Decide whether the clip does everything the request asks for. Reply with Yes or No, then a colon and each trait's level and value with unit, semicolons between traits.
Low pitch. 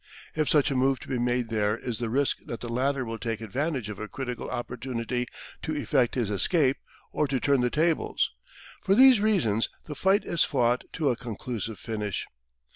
Yes: low, 125 Hz